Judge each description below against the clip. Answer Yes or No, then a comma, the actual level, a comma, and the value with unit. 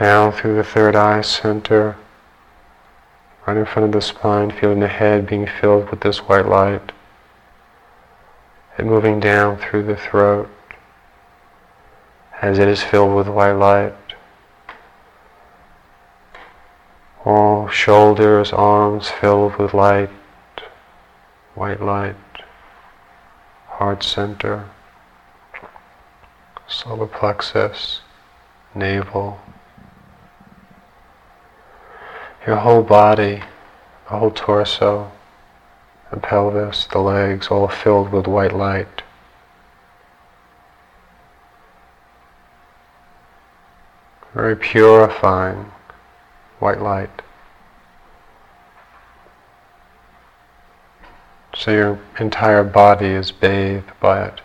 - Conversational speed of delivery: No, slow, 80 wpm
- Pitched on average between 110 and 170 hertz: No, low, 100 Hz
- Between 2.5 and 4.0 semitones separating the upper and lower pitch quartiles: Yes, average, 2.9 semitones